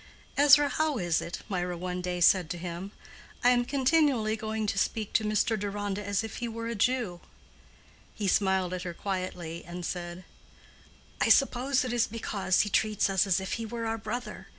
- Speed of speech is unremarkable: Yes, average, 185 wpm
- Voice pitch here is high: Yes, high, 205 Hz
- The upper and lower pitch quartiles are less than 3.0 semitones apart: No, average, 4.1 semitones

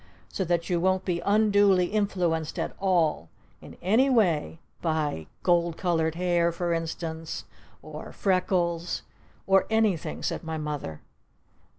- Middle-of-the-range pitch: Yes, medium, 175 Hz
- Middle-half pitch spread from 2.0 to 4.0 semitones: Yes, average, 2.8 semitones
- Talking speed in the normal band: No, slow, 130 wpm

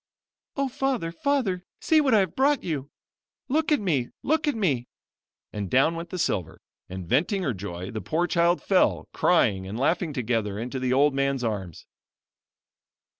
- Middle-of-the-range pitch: Yes, medium, 155 Hz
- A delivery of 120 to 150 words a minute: No, average, 170 wpm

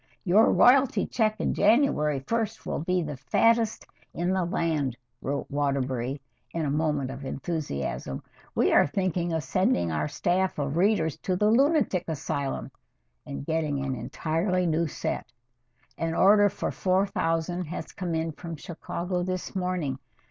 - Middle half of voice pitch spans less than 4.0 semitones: No, average, 4.7 semitones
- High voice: No, medium, 165 Hz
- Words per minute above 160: No, average, 150 wpm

